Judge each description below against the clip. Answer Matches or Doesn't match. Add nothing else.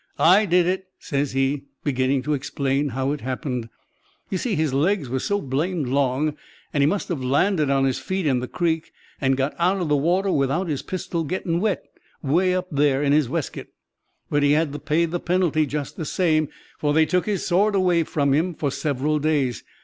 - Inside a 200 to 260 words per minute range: Matches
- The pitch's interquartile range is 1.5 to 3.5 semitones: Doesn't match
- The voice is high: Doesn't match